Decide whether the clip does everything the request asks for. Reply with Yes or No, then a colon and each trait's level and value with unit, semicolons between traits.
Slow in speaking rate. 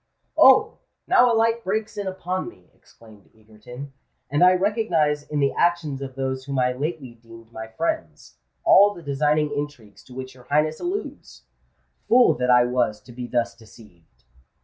No: average, 170 wpm